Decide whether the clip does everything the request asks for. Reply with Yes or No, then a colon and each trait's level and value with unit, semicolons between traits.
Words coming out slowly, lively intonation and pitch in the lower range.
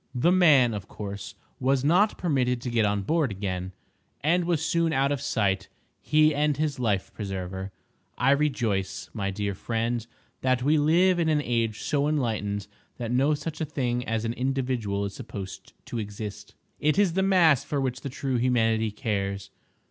No: average, 175 wpm; wide, 6.4 semitones; low, 125 Hz